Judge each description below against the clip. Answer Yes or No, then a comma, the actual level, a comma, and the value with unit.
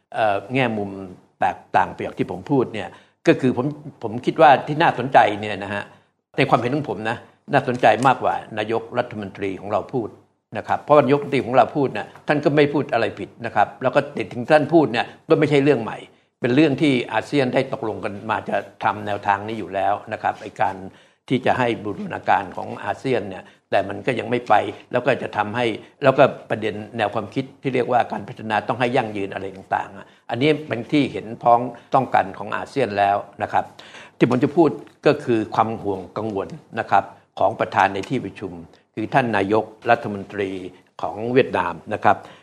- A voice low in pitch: Yes, low, 115 Hz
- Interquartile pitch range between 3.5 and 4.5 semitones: No, average, 4.9 semitones